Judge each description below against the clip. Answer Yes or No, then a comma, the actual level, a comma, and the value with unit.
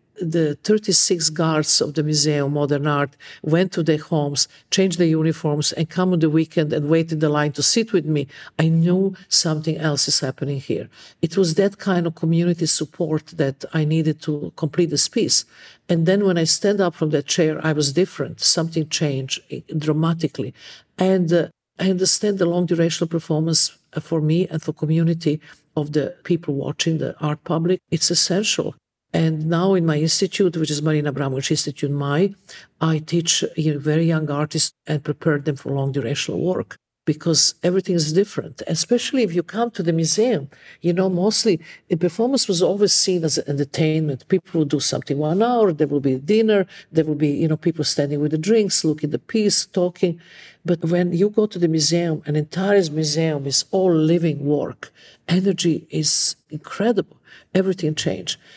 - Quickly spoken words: No, average, 180 wpm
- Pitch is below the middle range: No, medium, 160 Hz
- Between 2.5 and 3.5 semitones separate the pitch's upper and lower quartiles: Yes, average, 2.9 semitones